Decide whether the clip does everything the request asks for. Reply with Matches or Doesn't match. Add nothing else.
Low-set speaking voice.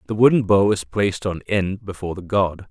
Matches